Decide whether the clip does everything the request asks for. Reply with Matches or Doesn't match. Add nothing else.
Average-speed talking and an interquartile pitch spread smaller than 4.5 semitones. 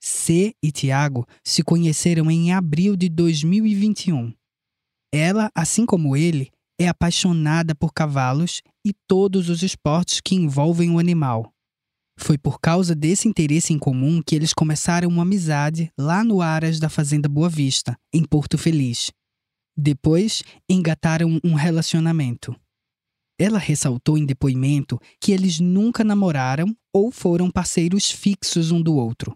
Matches